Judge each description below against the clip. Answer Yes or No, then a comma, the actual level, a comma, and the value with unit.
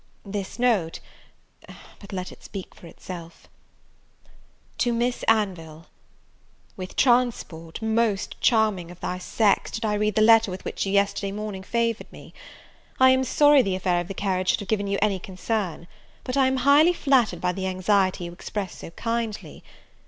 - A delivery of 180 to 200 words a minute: No, average, 165 wpm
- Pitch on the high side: Yes, high, 205 Hz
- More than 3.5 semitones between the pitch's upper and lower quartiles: Yes, average, 3.9 semitones